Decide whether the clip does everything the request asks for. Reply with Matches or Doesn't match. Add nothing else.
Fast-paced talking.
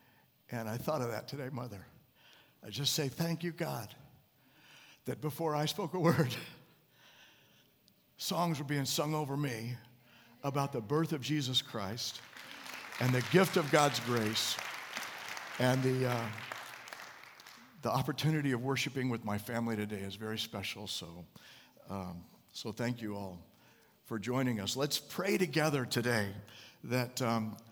Doesn't match